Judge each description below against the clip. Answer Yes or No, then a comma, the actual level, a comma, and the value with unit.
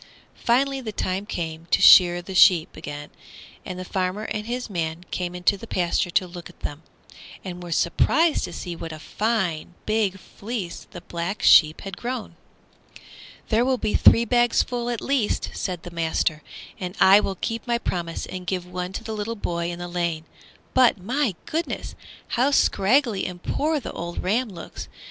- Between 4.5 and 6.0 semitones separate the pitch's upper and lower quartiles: Yes, average, 4.9 semitones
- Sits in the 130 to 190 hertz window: Yes, medium, 185 Hz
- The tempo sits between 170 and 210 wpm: Yes, average, 180 wpm